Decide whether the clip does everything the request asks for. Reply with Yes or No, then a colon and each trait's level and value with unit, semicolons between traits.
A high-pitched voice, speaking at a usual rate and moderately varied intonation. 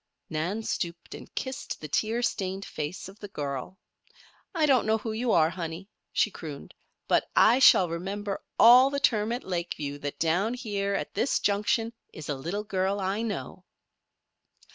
Yes: high, 195 Hz; average, 165 wpm; average, 4.7 semitones